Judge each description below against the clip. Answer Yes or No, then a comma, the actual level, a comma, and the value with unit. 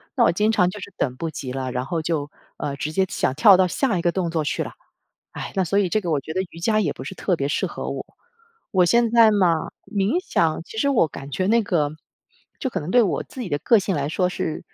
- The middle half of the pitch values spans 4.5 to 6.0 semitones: Yes, average, 5.0 semitones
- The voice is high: No, medium, 180 Hz